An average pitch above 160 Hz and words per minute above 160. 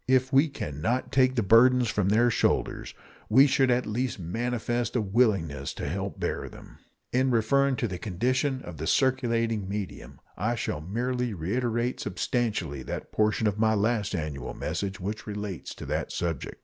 No: low, 110 Hz; average, 175 wpm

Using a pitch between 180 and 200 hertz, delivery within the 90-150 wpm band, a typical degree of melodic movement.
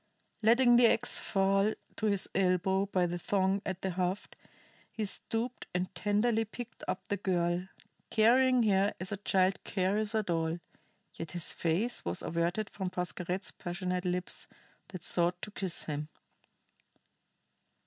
Yes: high, 190 Hz; average, 145 wpm; average, 3.0 semitones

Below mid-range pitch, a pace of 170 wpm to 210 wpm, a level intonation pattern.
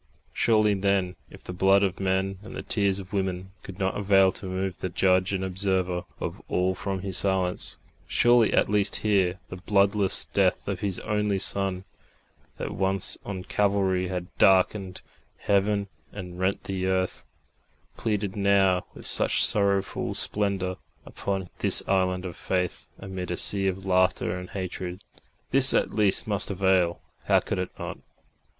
No: very low, 95 Hz; average, 155 wpm; narrow, 1.3 semitones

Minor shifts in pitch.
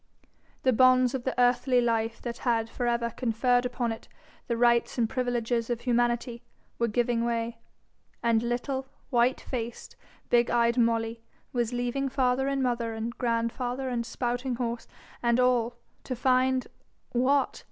Yes: narrow, 1.4 semitones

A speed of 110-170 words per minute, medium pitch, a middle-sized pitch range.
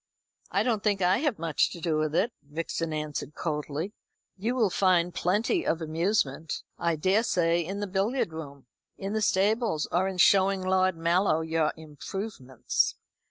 Yes: average, 160 wpm; medium, 175 Hz; average, 4.0 semitones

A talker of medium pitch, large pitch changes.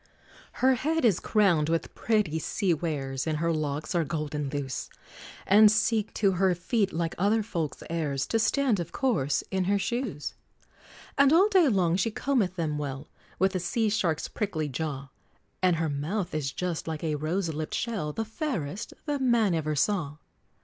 Yes: medium, 175 Hz; wide, 6.0 semitones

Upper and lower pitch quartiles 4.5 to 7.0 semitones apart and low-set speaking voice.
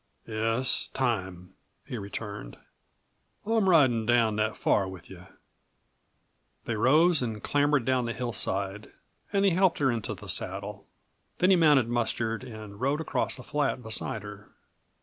Yes: average, 5.2 semitones; low, 120 Hz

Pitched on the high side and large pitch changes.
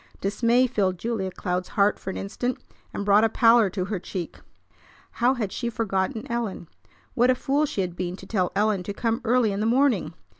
No: high, 210 Hz; average, 3.8 semitones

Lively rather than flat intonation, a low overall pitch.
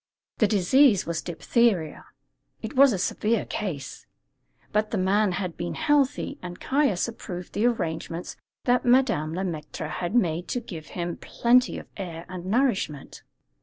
No: wide, 5.7 semitones; high, 195 Hz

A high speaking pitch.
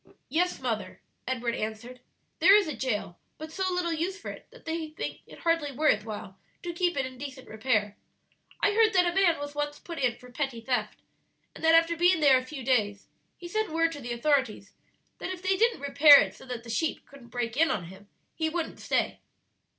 Yes: very high, 290 Hz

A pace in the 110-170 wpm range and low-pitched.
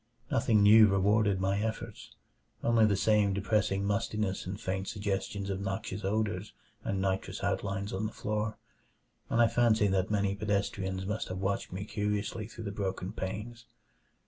Yes: average, 155 wpm; low, 100 Hz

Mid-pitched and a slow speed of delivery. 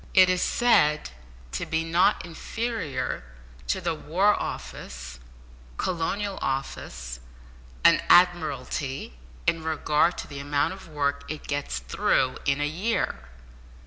Yes: medium, 155 Hz; slow, 120 wpm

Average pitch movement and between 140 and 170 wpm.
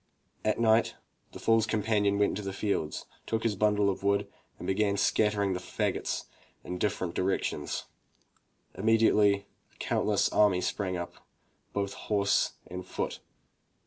No: narrow, 1.6 semitones; average, 145 wpm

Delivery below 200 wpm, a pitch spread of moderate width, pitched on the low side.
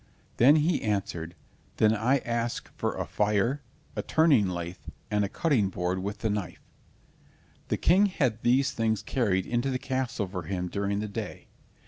Yes: average, 165 wpm; average, 4.8 semitones; low, 110 Hz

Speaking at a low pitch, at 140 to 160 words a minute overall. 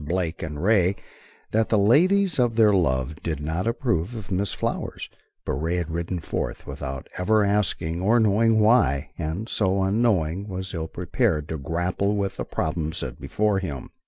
No: very low, 95 Hz; average, 170 wpm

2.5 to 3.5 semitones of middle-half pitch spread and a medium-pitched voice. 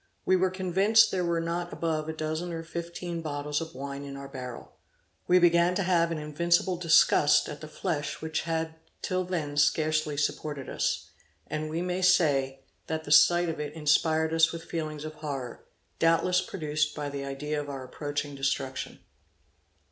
Yes: average, 2.8 semitones; medium, 160 Hz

